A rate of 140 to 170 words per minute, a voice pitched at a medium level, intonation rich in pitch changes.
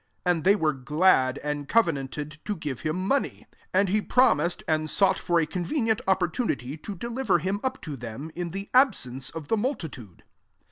No: average, 190 wpm; medium, 170 Hz; wide, 5.7 semitones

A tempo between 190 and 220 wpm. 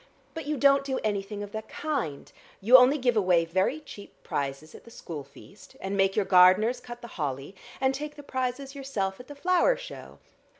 Yes: average, 200 wpm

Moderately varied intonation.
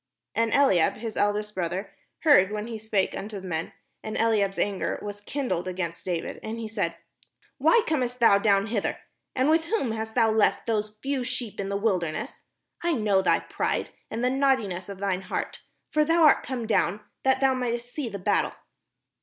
Yes: average, 4.1 semitones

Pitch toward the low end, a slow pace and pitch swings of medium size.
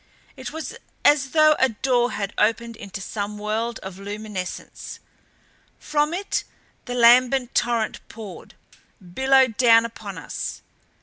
No: high, 230 Hz; slow, 125 wpm; average, 4.0 semitones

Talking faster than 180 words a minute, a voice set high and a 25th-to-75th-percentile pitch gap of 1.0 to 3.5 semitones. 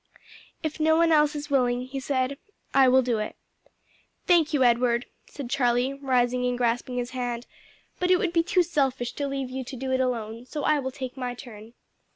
Yes: average, 200 wpm; very high, 260 Hz; average, 2.9 semitones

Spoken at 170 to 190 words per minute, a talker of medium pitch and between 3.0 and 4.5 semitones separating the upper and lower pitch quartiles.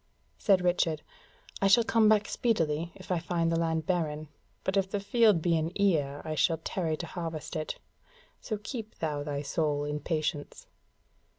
Yes: average, 175 wpm; medium, 165 Hz; average, 4.0 semitones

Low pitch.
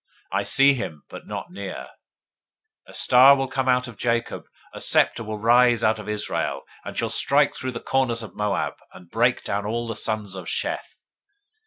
Yes: low, 115 Hz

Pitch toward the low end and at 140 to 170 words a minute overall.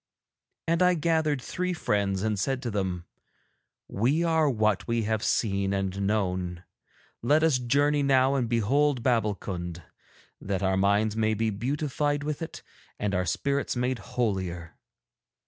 Yes: low, 115 Hz; average, 145 wpm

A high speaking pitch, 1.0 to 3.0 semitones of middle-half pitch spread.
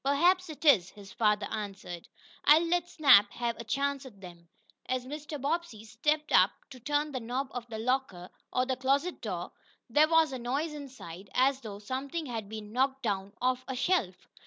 No: very high, 255 Hz; average, 5.2 semitones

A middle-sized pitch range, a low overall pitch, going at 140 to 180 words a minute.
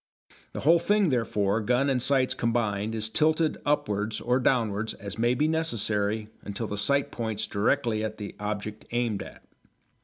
Yes: average, 3.8 semitones; low, 115 Hz; average, 160 wpm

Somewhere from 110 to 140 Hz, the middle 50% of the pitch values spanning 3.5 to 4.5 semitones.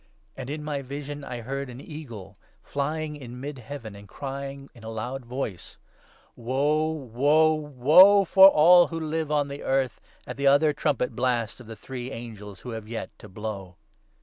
Yes: low, 135 Hz; average, 4.1 semitones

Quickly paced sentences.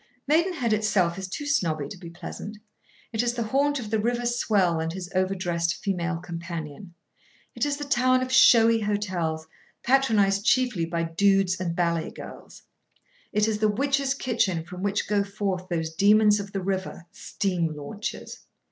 No: average, 160 wpm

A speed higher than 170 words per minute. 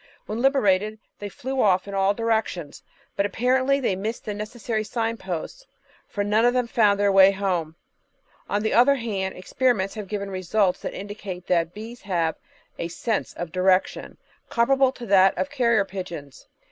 No: average, 165 wpm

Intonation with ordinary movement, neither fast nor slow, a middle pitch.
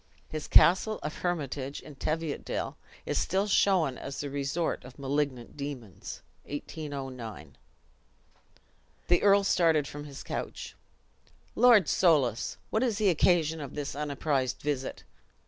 No: average, 4.0 semitones; slow, 125 wpm; medium, 150 Hz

